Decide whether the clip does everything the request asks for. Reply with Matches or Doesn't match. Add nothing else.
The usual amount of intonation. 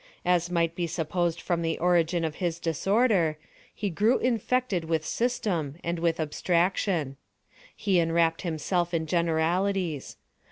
Doesn't match